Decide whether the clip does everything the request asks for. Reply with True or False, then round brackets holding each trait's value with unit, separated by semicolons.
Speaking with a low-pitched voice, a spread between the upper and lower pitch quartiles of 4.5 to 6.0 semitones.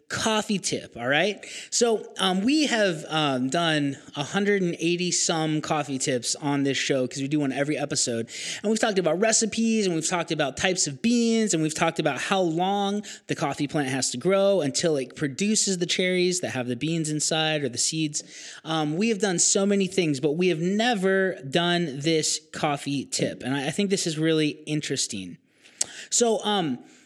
False (165 Hz; 5.1 semitones)